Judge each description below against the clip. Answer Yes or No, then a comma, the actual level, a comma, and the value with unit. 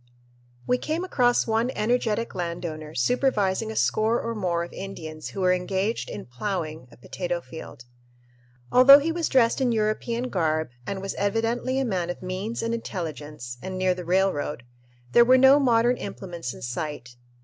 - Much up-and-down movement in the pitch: Yes, wide, 5.7 semitones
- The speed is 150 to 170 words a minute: Yes, average, 165 wpm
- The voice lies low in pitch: No, high, 195 Hz